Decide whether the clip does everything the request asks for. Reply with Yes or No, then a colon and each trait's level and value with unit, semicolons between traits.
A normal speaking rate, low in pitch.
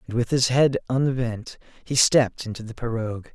Yes: average, 180 wpm; low, 120 Hz